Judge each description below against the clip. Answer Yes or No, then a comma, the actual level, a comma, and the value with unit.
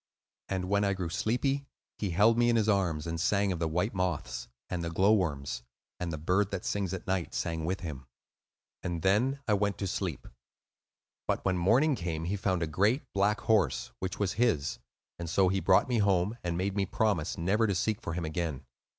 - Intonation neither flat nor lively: Yes, average, 3.5 semitones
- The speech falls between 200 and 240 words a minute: Yes, fast, 205 wpm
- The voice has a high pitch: No, very low, 95 Hz